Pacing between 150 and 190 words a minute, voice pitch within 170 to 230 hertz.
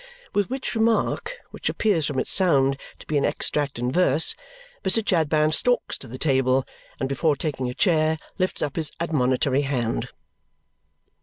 No: average, 160 wpm; medium, 150 Hz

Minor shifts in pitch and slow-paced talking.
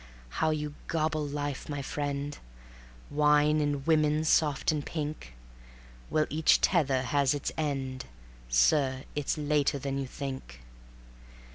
Yes: narrow, 1.7 semitones; slow, 125 wpm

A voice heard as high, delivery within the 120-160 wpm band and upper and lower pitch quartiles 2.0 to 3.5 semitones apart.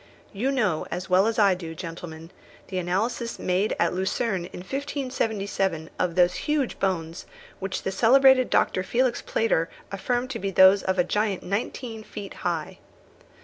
No: high, 195 Hz; average, 155 wpm; average, 4.5 semitones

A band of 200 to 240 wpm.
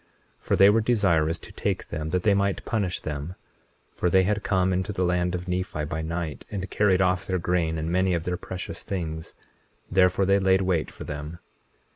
Yes: fast, 205 wpm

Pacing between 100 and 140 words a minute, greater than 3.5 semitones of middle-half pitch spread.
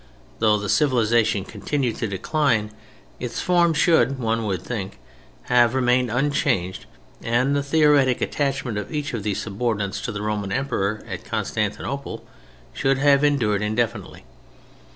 Yes: slow, 135 wpm; average, 4.6 semitones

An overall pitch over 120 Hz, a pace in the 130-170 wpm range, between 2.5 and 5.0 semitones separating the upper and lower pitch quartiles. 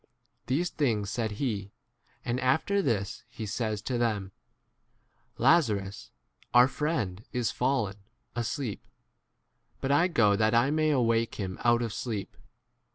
No: low, 115 Hz; slow, 135 wpm; average, 4.3 semitones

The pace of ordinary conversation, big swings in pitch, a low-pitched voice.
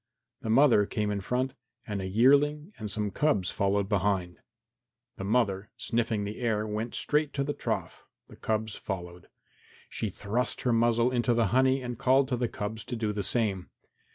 No: average, 180 wpm; average, 3.5 semitones; low, 110 Hz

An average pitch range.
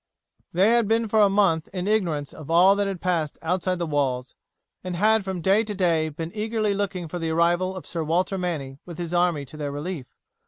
Yes: average, 3.5 semitones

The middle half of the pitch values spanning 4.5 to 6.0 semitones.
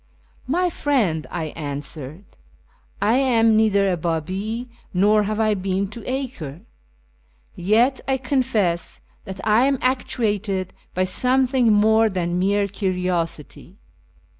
Yes: average, 5.1 semitones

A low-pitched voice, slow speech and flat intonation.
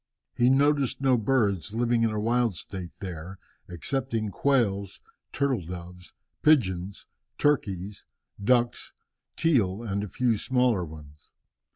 No: low, 110 Hz; slow, 115 wpm; average, 5.2 semitones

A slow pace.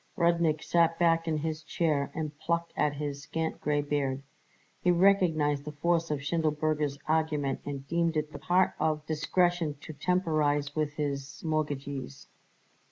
No: average, 150 wpm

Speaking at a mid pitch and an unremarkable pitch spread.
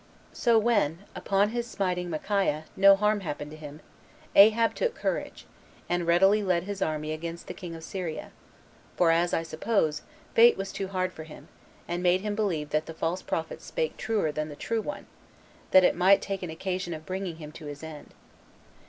Yes: medium, 180 Hz; average, 3.9 semitones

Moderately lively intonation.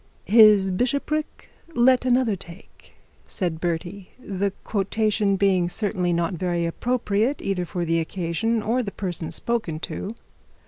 Yes: average, 4.4 semitones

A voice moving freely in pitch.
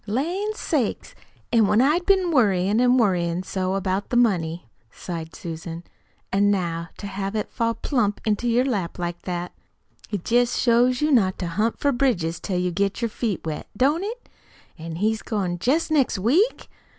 Yes: wide, 5.7 semitones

